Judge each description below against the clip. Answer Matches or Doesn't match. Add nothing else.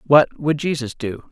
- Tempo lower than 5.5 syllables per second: Matches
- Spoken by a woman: Doesn't match